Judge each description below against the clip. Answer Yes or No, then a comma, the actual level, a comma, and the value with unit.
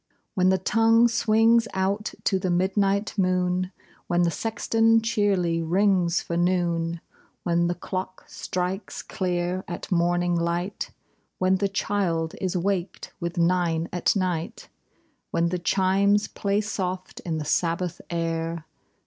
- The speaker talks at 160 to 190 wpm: No, average, 145 wpm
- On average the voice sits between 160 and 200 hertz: Yes, medium, 185 Hz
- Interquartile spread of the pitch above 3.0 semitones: No, narrow, 2.5 semitones